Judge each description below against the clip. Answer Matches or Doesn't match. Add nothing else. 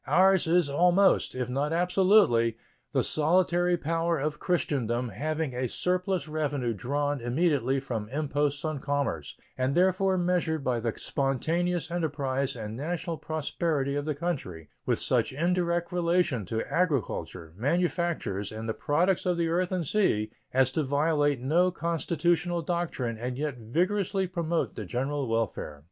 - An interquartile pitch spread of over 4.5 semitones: Matches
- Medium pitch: Matches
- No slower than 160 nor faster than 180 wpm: Doesn't match